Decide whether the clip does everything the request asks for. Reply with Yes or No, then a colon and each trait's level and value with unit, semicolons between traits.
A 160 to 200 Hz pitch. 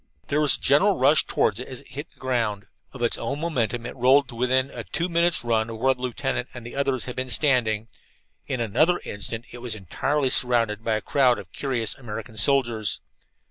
No: low, 125 Hz